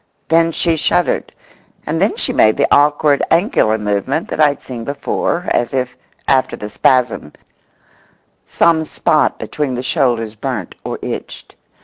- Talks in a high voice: No, low, 135 Hz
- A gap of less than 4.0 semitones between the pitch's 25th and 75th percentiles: No, average, 5.0 semitones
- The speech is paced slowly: No, average, 145 wpm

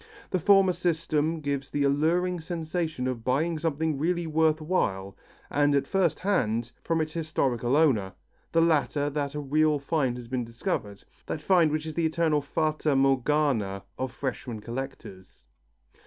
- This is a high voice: No, medium, 150 Hz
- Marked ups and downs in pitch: No, average, 3.8 semitones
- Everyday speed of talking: Yes, average, 155 wpm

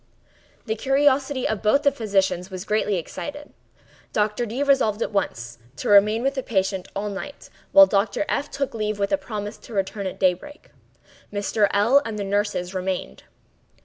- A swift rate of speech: No, average, 170 wpm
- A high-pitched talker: Yes, high, 210 Hz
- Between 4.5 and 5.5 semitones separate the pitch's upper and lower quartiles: Yes, average, 5.1 semitones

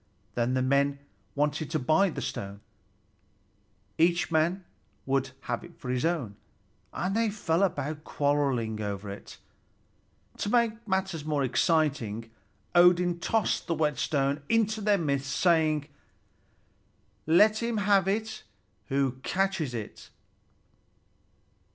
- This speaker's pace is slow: Yes, slow, 120 wpm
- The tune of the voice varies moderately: No, wide, 5.9 semitones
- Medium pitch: Yes, medium, 155 Hz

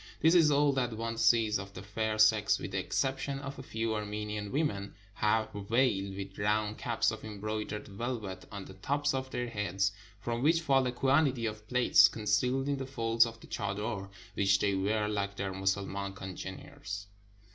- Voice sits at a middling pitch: No, low, 110 Hz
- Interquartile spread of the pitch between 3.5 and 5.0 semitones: Yes, average, 4.0 semitones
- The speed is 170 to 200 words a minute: Yes, average, 180 wpm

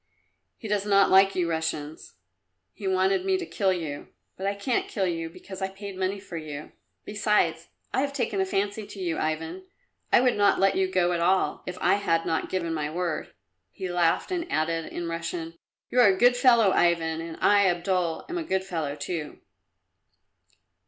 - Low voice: No, medium, 185 Hz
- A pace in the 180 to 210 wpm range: Yes, average, 195 wpm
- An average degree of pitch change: Yes, average, 3.4 semitones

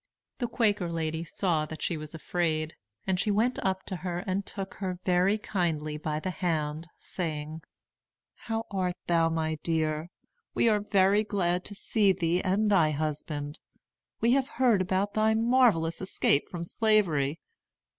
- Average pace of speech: Yes, average, 155 wpm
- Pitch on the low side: No, medium, 180 Hz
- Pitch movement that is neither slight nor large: Yes, average, 4.4 semitones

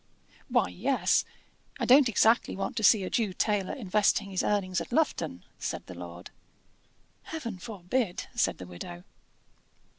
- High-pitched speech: Yes, high, 200 Hz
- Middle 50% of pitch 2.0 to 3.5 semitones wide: No, average, 4.8 semitones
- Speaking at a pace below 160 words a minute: Yes, average, 145 wpm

